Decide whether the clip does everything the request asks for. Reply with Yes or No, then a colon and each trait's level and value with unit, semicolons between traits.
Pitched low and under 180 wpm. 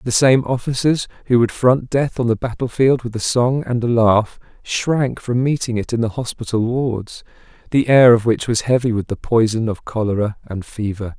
No: low, 120 Hz; average, 200 wpm